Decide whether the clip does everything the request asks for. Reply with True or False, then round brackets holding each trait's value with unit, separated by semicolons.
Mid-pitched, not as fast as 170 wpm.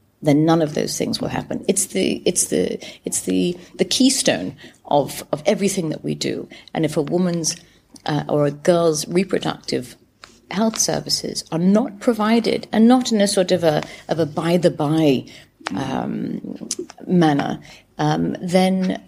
True (175 Hz; 155 wpm)